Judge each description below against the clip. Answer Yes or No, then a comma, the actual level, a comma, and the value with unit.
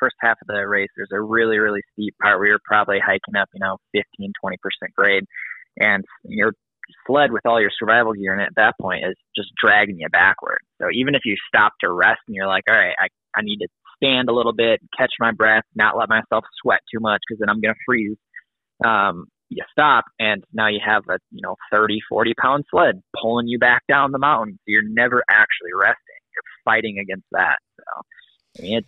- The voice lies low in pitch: Yes, low, 110 Hz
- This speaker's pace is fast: Yes, fast, 220 wpm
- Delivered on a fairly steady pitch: Yes, narrow, 1.9 semitones